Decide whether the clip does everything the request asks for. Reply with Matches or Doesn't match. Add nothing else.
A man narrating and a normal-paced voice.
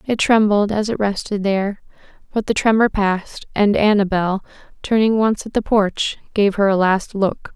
Doesn't match